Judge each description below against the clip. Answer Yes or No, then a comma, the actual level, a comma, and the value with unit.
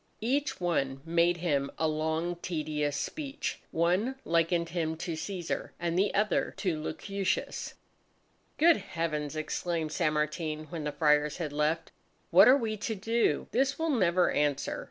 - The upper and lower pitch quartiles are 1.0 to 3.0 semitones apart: No, average, 3.8 semitones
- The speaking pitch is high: No, medium, 170 Hz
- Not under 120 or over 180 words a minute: Yes, average, 150 wpm